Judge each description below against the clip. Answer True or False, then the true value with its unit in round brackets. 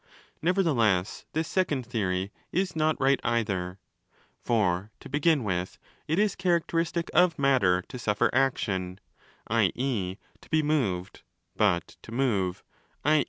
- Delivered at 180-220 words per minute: False (140 wpm)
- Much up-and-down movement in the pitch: True (8.6 semitones)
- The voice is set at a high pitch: False (125 Hz)